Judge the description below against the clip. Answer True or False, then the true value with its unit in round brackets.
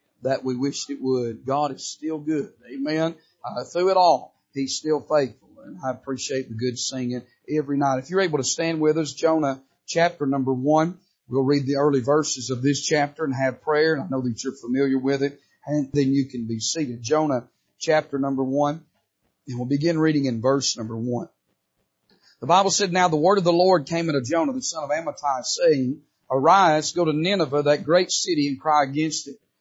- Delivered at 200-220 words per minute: True (205 wpm)